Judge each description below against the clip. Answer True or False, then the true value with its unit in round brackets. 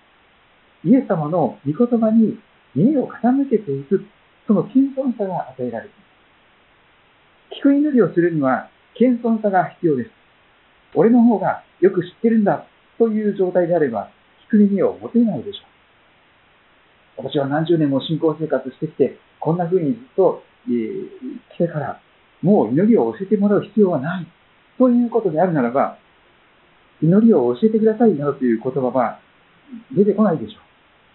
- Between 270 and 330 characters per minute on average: True (310 characters per minute)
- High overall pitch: True (200 Hz)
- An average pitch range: False (6.7 semitones)